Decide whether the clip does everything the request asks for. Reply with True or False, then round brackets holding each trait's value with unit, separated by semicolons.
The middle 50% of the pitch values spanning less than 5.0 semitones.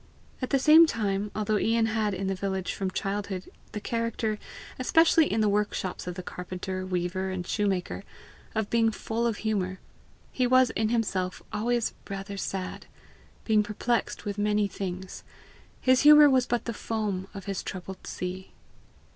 True (3.3 semitones)